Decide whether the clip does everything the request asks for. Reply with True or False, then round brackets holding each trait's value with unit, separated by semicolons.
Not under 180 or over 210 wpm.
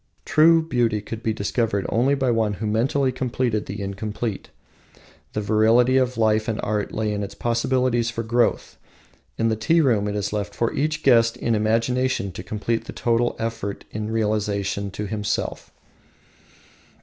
False (160 wpm)